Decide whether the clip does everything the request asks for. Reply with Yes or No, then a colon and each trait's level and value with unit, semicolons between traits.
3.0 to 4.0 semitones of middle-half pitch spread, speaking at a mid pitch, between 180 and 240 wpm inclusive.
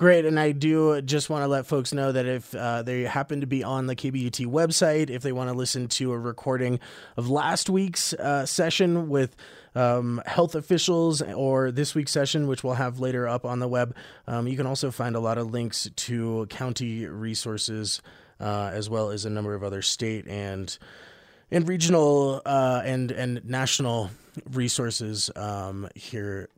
No: average, 3.7 semitones; low, 125 Hz; average, 185 wpm